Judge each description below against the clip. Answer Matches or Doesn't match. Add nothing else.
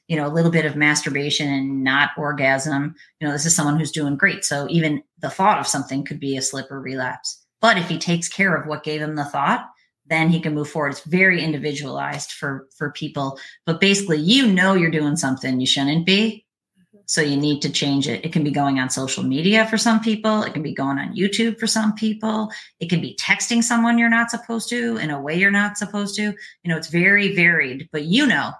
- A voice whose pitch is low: Doesn't match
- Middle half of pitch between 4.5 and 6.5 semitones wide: Matches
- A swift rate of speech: Matches